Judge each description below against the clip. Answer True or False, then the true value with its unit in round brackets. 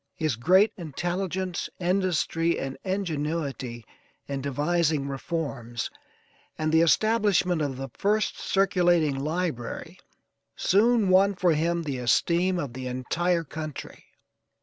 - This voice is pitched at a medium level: True (165 Hz)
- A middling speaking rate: False (110 wpm)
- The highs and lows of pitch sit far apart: False (4.7 semitones)